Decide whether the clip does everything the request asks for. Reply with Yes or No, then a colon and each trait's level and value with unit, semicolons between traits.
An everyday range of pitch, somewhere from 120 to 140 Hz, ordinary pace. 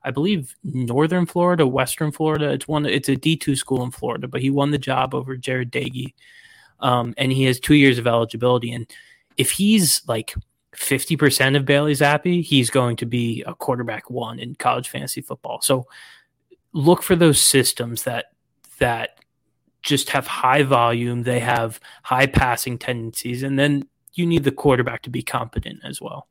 Yes: average, 3.4 semitones; low, 135 Hz; average, 180 wpm